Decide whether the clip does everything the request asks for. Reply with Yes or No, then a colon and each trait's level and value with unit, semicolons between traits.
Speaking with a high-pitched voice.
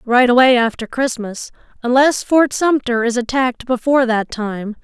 Yes: high, 245 Hz